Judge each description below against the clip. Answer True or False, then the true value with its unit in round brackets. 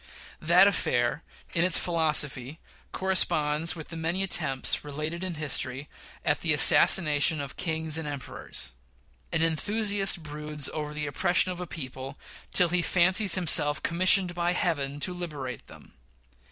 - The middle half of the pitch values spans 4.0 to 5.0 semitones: False (3.3 semitones)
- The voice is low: False (160 Hz)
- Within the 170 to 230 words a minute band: False (140 wpm)